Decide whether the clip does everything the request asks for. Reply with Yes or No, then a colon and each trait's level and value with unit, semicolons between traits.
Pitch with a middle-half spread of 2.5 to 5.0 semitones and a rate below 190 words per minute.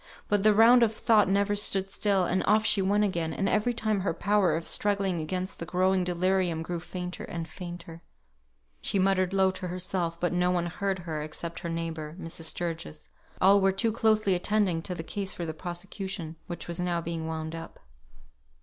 No: average, 2.8 semitones; average, 195 wpm